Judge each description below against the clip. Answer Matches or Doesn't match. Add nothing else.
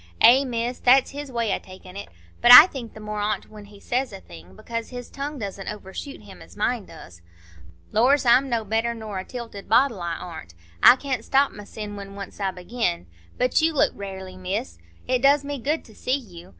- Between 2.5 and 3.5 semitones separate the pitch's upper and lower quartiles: Doesn't match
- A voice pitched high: Matches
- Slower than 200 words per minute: Doesn't match